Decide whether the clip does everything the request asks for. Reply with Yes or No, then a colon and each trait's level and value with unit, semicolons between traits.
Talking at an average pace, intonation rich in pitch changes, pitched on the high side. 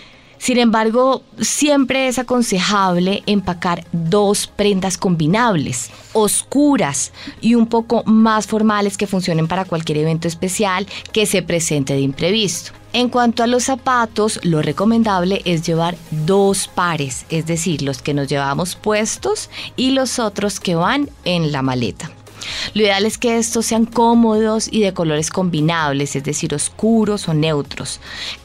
Yes: average, 145 wpm; wide, 5.8 semitones; high, 195 Hz